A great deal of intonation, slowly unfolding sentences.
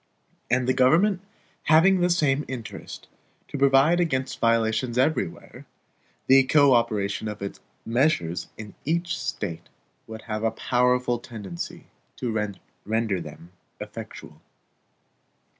No: average, 4.4 semitones; slow, 115 wpm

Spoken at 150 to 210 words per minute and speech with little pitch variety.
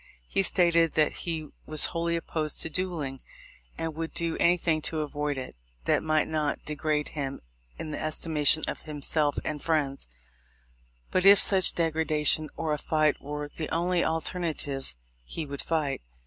Yes: average, 160 wpm; narrow, 2.0 semitones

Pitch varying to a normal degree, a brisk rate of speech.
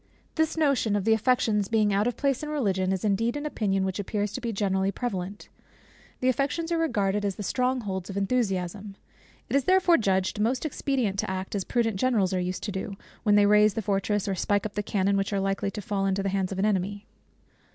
Yes: average, 3.6 semitones; fast, 225 wpm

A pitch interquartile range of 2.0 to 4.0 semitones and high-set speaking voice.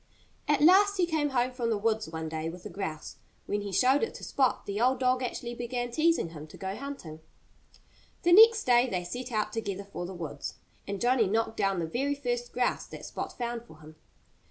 No: wide, 5.4 semitones; high, 235 Hz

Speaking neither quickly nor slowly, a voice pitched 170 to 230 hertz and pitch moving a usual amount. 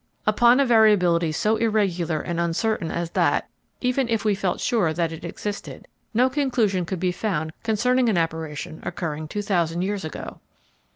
Yes: average, 160 wpm; high, 190 Hz; average, 4.9 semitones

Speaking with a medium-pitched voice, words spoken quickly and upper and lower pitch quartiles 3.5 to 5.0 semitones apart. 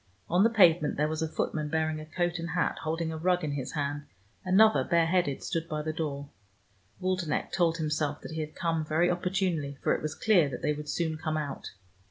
No: medium, 160 Hz; fast, 215 wpm; narrow, 2.5 semitones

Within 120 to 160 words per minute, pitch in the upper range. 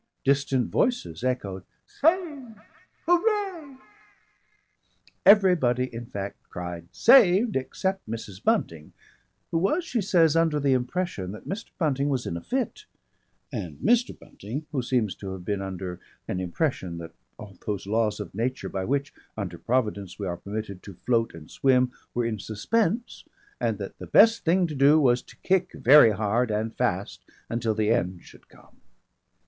No: average, 155 wpm; low, 125 Hz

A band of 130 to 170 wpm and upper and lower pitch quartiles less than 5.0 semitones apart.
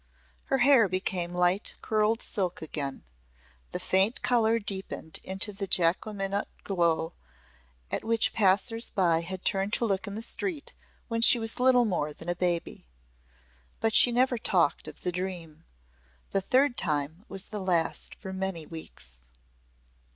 Yes: average, 150 wpm; average, 4.4 semitones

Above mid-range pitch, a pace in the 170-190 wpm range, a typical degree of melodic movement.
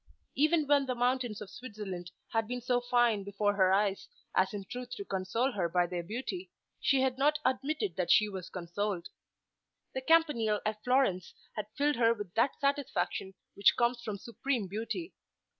Yes: high, 230 Hz; average, 175 wpm; average, 4.8 semitones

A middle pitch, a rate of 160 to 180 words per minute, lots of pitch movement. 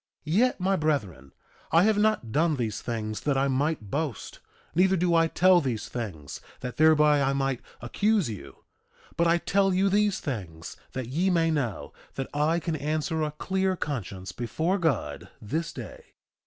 Yes: medium, 150 Hz; average, 170 wpm; wide, 6.5 semitones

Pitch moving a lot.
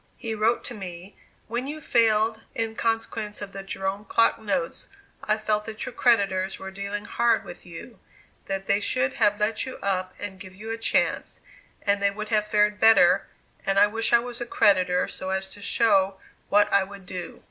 No: narrow, 2.5 semitones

